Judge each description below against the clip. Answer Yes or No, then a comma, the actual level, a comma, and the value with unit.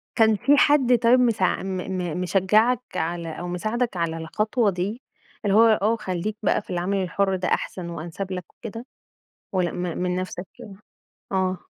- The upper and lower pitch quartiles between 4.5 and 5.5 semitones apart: No, average, 3.7 semitones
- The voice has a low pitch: No, high, 190 Hz